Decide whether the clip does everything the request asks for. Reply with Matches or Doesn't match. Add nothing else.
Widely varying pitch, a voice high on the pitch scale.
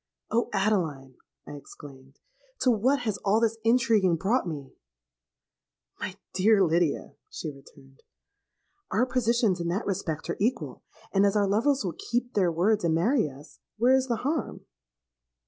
Matches